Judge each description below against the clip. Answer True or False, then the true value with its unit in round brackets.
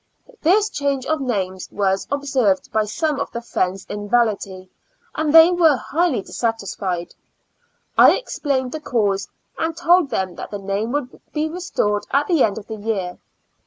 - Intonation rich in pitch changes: True (7.3 semitones)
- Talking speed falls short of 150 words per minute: False (160 wpm)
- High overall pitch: True (240 Hz)